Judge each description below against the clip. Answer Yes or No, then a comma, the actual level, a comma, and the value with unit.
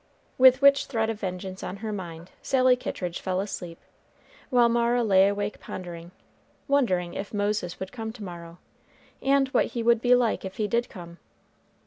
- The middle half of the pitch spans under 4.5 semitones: No, average, 4.8 semitones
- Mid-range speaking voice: No, high, 210 Hz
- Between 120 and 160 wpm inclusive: No, average, 170 wpm